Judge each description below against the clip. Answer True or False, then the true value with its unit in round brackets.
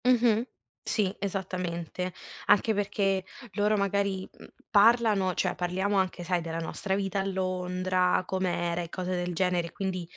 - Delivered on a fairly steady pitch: True (1.8 semitones)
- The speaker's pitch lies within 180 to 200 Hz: True (185 Hz)